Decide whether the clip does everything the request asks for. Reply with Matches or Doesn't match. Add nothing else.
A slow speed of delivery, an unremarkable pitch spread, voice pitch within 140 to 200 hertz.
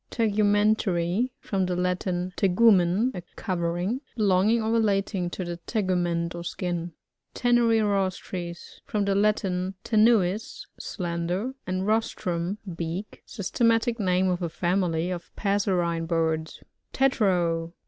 Matches